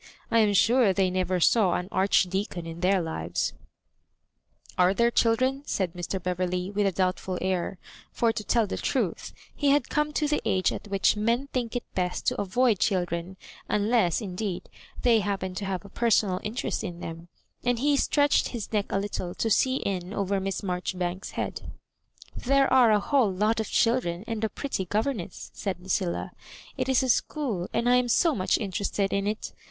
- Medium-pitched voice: No, high, 200 Hz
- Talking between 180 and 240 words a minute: Yes, average, 190 wpm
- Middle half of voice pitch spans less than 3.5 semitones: No, average, 4.3 semitones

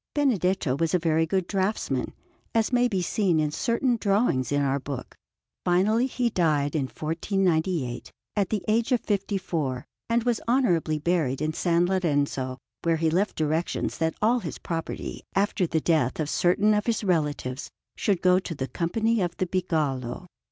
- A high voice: No, medium, 175 Hz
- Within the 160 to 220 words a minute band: Yes, average, 170 wpm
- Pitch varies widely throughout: No, average, 5.0 semitones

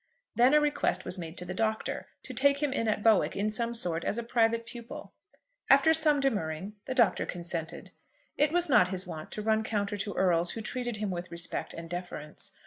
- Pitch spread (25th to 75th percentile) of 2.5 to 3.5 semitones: No, average, 5.3 semitones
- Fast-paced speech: Yes, fast, 210 wpm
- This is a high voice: Yes, high, 215 Hz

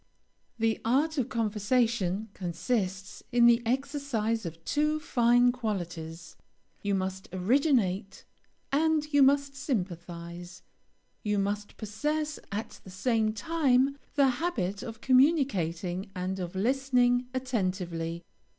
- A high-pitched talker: Yes, high, 225 Hz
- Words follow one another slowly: Yes, slow, 110 wpm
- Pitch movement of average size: No, wide, 5.9 semitones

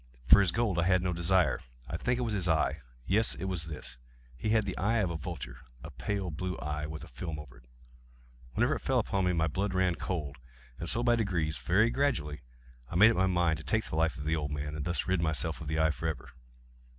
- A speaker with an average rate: No, fast, 235 wpm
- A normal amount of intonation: Yes, average, 3.9 semitones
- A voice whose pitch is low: Yes, very low, 85 Hz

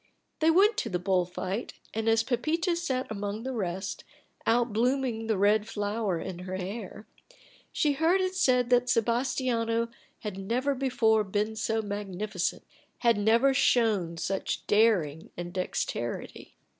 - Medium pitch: No, high, 220 Hz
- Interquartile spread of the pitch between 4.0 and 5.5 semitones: Yes, average, 4.3 semitones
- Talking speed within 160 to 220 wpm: No, average, 145 wpm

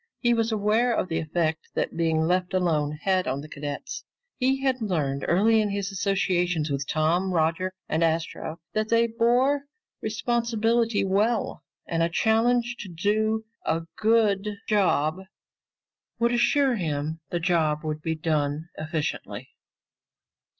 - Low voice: No, medium, 185 Hz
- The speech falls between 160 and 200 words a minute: No, average, 140 wpm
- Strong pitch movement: Yes, wide, 5.9 semitones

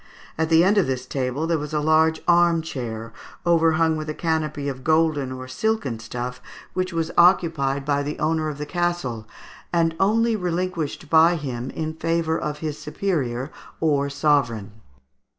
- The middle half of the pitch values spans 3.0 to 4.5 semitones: Yes, average, 3.4 semitones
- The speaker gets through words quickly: No, average, 165 wpm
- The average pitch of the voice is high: No, medium, 155 Hz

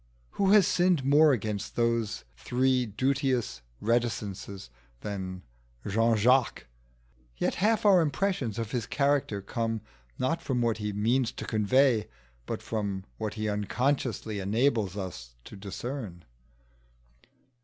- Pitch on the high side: No, low, 115 Hz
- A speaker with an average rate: No, slow, 120 wpm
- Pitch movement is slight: No, average, 4.6 semitones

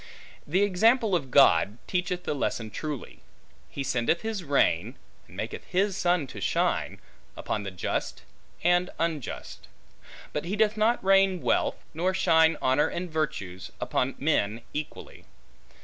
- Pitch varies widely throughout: Yes, wide, 5.7 semitones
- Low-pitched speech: No, medium, 165 Hz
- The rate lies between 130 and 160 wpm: Yes, average, 140 wpm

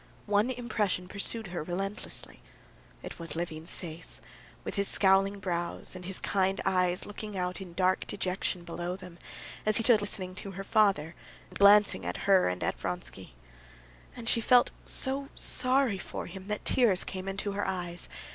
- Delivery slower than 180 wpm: Yes, average, 165 wpm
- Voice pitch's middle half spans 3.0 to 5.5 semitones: No, narrow, 2.5 semitones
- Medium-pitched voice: No, high, 195 Hz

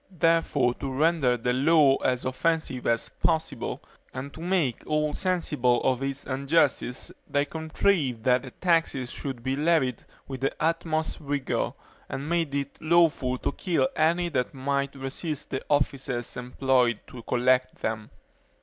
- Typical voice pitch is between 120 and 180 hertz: Yes, medium, 140 Hz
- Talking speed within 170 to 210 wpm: No, average, 145 wpm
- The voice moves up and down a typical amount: Yes, average, 3.9 semitones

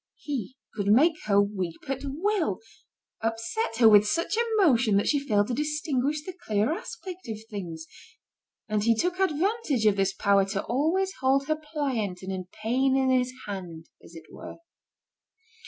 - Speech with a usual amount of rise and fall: No, wide, 7.1 semitones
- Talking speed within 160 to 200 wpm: Yes, average, 165 wpm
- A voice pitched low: No, very high, 250 Hz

